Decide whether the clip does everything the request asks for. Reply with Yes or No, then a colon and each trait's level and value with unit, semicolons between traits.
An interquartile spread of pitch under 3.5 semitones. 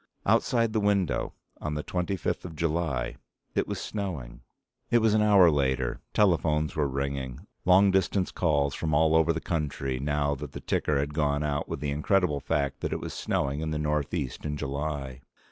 No: average, 4.0 semitones